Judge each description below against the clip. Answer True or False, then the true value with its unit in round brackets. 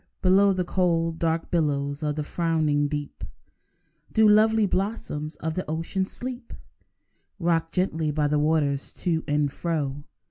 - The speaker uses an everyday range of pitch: True (3.7 semitones)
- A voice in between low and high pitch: True (165 Hz)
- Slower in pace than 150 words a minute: True (140 wpm)